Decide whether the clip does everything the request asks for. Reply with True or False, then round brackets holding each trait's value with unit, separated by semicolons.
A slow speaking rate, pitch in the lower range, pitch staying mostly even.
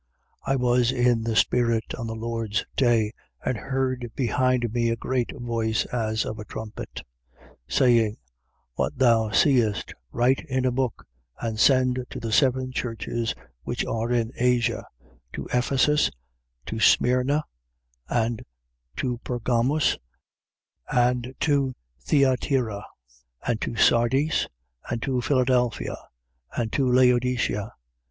True (130 wpm; 120 Hz; 2.2 semitones)